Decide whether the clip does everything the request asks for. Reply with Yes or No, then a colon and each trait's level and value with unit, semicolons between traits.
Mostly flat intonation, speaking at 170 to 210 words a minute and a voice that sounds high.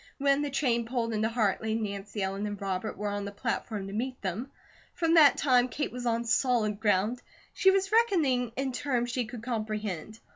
No: average, 3.7 semitones; average, 190 wpm; high, 230 Hz